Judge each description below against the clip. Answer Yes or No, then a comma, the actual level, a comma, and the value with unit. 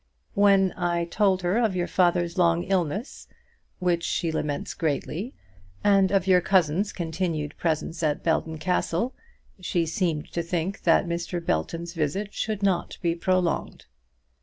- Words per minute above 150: No, average, 140 wpm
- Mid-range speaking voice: Yes, medium, 175 Hz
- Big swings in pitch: No, narrow, 2.4 semitones